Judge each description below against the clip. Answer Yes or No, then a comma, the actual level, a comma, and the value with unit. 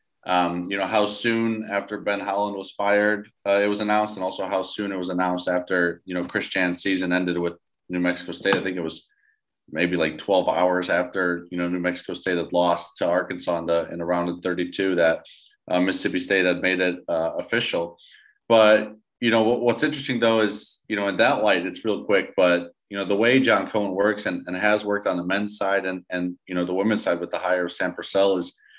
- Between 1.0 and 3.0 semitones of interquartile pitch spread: Yes, average, 2.7 semitones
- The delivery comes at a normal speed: No, fast, 225 wpm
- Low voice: Yes, very low, 95 Hz